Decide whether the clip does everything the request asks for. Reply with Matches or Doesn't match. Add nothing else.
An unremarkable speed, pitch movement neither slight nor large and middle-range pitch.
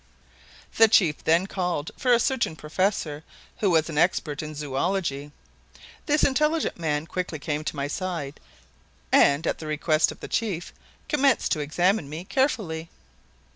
Matches